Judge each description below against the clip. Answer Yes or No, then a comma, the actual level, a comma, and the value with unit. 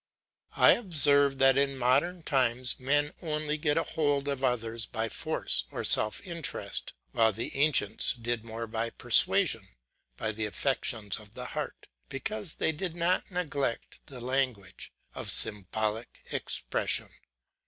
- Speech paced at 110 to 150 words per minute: Yes, average, 140 wpm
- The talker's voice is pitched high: No, low, 135 Hz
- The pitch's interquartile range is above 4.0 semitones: Yes, average, 4.6 semitones